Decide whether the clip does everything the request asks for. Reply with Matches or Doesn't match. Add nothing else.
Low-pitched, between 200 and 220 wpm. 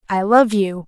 Doesn't match